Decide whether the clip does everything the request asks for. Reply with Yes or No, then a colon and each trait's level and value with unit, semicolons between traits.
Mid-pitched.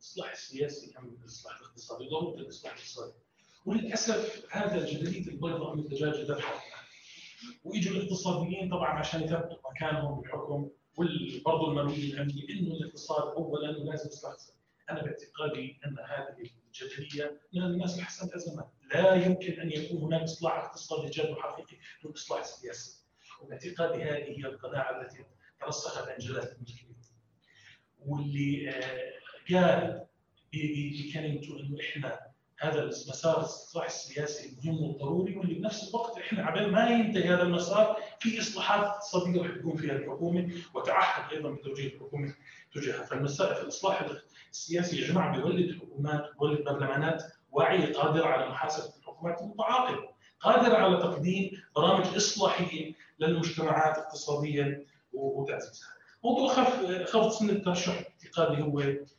Yes: medium, 160 Hz